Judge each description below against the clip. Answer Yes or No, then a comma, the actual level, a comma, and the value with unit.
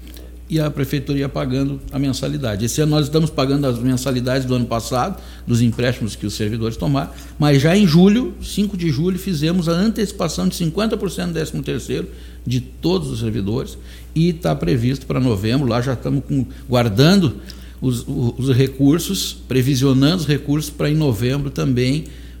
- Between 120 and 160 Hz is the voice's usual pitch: Yes, low, 135 Hz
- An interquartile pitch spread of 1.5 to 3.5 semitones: No, average, 4.3 semitones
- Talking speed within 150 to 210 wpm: Yes, average, 165 wpm